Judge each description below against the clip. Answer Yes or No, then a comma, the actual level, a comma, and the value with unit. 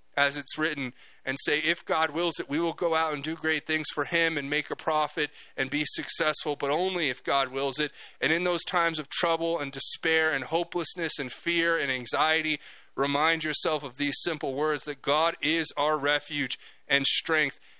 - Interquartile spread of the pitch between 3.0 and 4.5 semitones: No, narrow, 2.5 semitones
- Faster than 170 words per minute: Yes, average, 200 wpm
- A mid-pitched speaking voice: Yes, medium, 155 Hz